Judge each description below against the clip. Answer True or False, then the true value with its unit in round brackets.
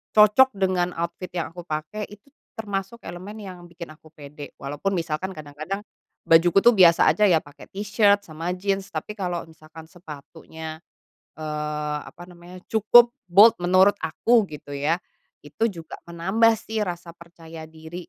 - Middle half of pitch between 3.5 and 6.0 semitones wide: True (3.9 semitones)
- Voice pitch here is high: False (175 Hz)